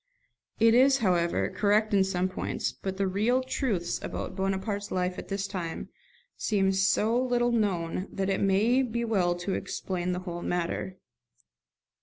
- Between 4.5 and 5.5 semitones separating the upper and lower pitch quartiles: No, average, 3.2 semitones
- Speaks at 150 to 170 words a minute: Yes, average, 155 wpm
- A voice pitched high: Yes, high, 195 Hz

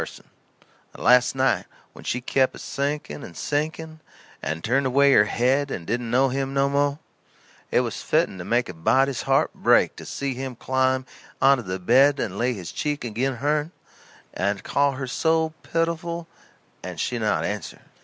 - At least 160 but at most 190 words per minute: Yes, average, 175 wpm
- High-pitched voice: No, low, 135 Hz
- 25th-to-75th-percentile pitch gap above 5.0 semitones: No, average, 3.0 semitones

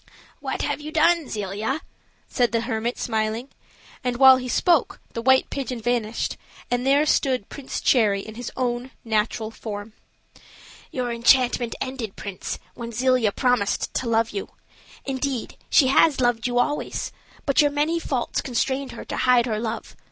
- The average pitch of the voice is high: Yes, high, 245 Hz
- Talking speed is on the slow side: No, average, 160 wpm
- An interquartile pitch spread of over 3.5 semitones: No, average, 2.9 semitones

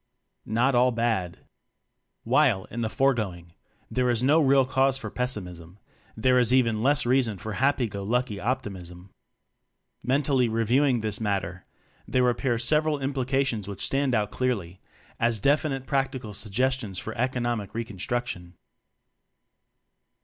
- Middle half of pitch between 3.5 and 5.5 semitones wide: Yes, average, 4.1 semitones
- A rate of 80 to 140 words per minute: Yes, slow, 135 wpm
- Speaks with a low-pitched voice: Yes, low, 120 Hz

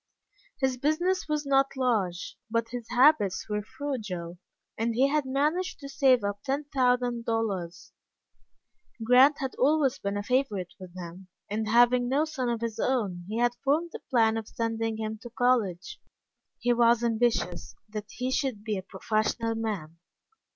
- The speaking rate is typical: Yes, average, 160 wpm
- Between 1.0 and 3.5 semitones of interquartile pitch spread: No, average, 4.0 semitones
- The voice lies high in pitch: Yes, high, 235 Hz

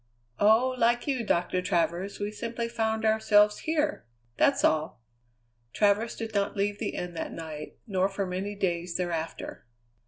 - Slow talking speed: No, average, 150 wpm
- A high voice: Yes, high, 205 Hz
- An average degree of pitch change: Yes, average, 4.0 semitones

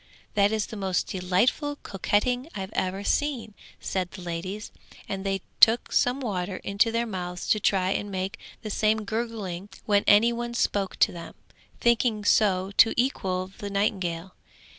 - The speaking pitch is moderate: No, high, 200 Hz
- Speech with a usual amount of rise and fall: Yes, average, 3.2 semitones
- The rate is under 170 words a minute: Yes, average, 160 wpm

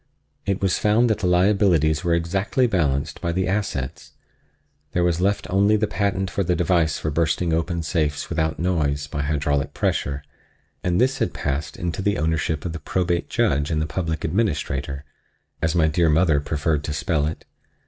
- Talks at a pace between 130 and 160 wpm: No, average, 175 wpm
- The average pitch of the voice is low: Yes, very low, 85 Hz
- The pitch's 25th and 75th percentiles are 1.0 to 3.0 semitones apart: No, average, 3.8 semitones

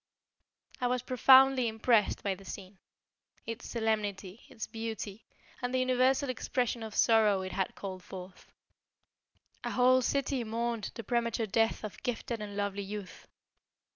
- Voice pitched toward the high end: Yes, high, 225 Hz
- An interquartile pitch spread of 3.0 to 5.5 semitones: Yes, average, 3.4 semitones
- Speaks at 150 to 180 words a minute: No, average, 140 wpm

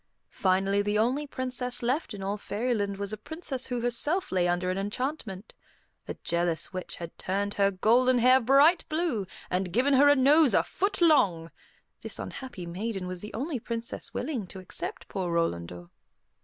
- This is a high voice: Yes, high, 215 Hz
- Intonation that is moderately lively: No, wide, 5.7 semitones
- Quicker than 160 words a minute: Yes, average, 170 wpm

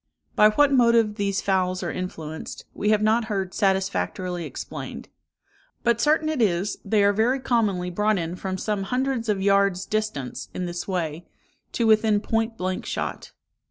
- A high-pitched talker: Yes, high, 205 Hz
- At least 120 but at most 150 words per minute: No, average, 160 wpm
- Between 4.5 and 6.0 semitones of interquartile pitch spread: No, average, 3.4 semitones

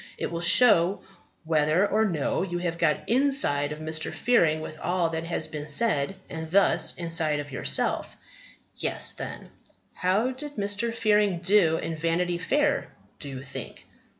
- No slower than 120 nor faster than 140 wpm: No, average, 155 wpm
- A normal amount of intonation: Yes, average, 4.6 semitones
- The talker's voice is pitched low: No, medium, 170 Hz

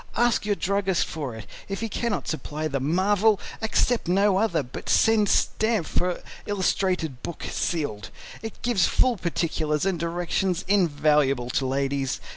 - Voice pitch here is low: No, medium, 175 Hz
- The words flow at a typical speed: Yes, average, 145 wpm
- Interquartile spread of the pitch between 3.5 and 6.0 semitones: Yes, wide, 5.4 semitones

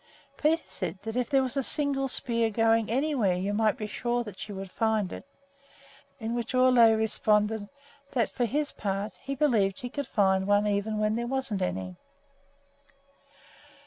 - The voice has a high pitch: Yes, high, 225 Hz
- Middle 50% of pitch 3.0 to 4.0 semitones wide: Yes, average, 3.6 semitones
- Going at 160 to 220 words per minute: Yes, average, 175 wpm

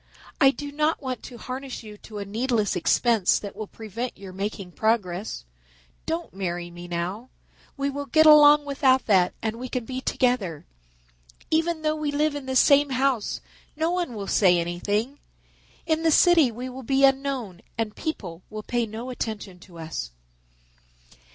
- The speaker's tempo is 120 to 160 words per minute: No, average, 170 wpm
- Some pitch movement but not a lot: No, wide, 5.9 semitones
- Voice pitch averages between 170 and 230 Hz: No, high, 240 Hz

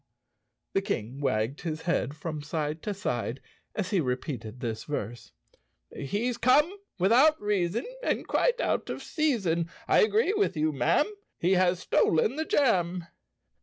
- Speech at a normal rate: Yes, average, 150 wpm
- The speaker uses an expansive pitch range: Yes, wide, 7.0 semitones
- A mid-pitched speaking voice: Yes, medium, 175 Hz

